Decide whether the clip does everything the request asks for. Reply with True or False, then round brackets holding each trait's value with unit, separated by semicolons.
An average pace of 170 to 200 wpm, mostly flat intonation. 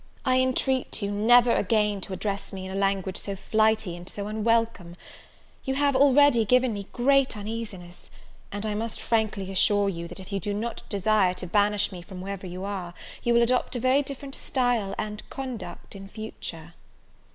False (185 wpm; 3.5 semitones)